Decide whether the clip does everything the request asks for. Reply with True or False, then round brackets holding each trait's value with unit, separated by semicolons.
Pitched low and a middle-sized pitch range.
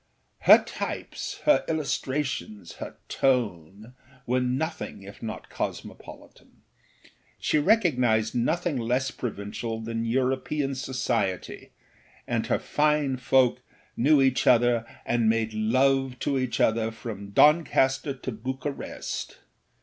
True (125 Hz; 3.3 semitones)